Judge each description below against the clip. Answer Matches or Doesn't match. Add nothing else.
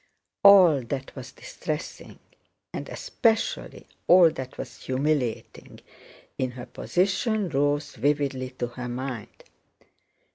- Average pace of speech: Doesn't match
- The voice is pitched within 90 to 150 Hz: Matches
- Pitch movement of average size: Matches